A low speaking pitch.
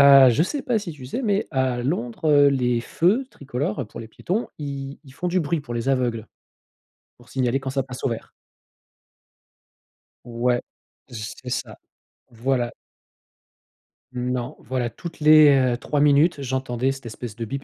Yes: low, 130 Hz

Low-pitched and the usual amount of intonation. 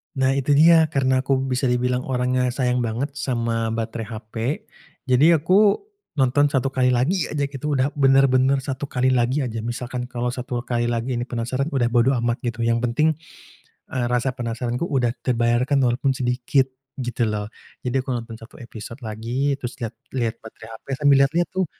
No: low, 125 Hz; narrow, 2.3 semitones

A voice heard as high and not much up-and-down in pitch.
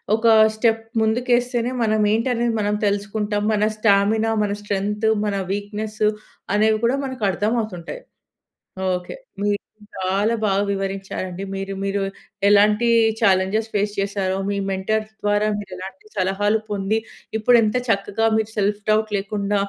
Yes: high, 205 Hz; narrow, 1.8 semitones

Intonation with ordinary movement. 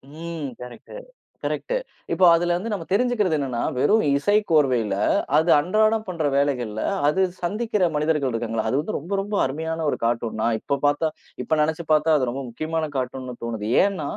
No: wide, 6.2 semitones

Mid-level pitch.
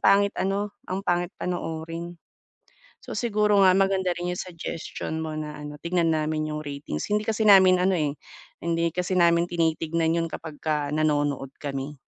Yes: medium, 170 Hz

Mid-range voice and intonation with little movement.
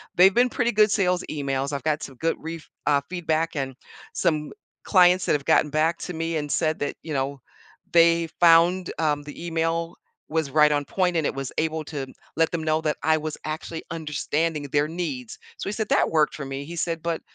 Yes: medium, 160 Hz; narrow, 2.2 semitones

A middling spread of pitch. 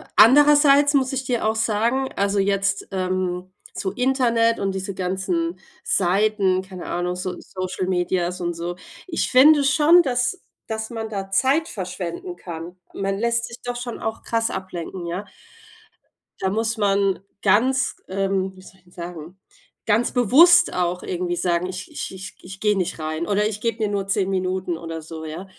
Yes: average, 4.3 semitones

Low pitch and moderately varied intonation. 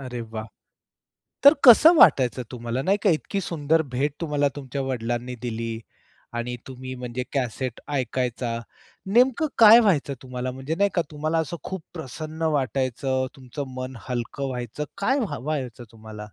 Yes: low, 130 Hz; average, 4.5 semitones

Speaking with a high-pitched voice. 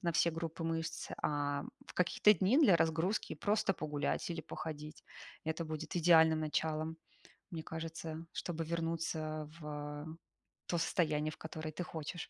No: medium, 160 Hz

